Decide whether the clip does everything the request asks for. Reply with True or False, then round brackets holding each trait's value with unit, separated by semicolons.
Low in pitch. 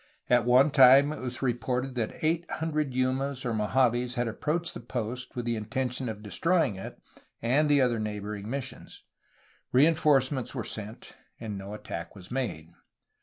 True (125 Hz)